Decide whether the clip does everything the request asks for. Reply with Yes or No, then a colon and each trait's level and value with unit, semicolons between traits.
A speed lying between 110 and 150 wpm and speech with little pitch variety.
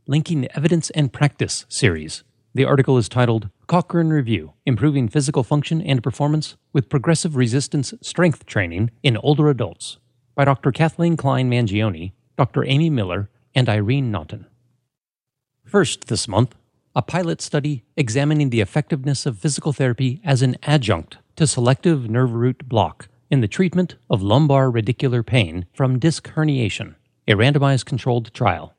No: average, 145 wpm; average, 3.9 semitones